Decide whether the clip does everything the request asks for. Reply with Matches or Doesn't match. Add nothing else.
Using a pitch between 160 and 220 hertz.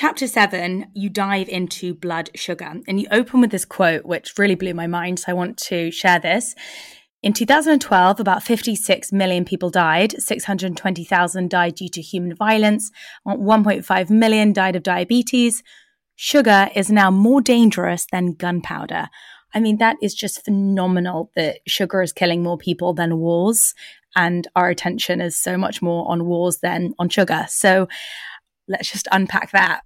Matches